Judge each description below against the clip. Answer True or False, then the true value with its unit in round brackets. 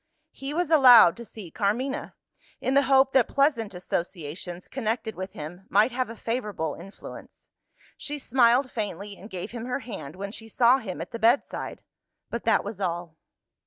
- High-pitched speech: True (225 Hz)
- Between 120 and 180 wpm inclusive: True (170 wpm)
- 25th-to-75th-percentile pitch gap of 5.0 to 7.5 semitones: True (5.3 semitones)